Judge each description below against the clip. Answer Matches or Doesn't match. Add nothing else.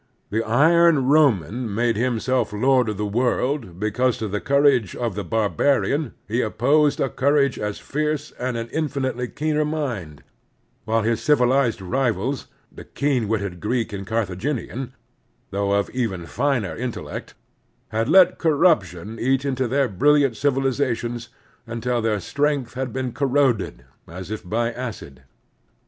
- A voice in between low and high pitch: Doesn't match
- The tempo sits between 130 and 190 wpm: Matches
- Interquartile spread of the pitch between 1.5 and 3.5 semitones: Doesn't match